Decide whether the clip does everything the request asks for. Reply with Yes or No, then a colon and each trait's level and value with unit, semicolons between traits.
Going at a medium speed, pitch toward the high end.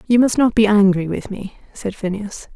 No: fast, 210 wpm; high, 210 Hz